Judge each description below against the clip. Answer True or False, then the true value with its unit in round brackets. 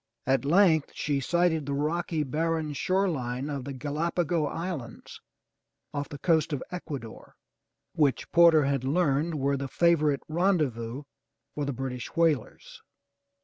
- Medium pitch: True (150 Hz)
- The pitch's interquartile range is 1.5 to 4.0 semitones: True (3.4 semitones)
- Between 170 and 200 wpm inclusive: False (145 wpm)